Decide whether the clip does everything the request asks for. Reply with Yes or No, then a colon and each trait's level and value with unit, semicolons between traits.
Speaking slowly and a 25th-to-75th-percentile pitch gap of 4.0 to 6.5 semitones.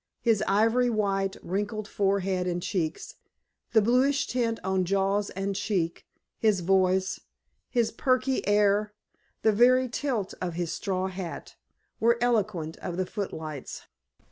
No: slow, 130 wpm; average, 3.5 semitones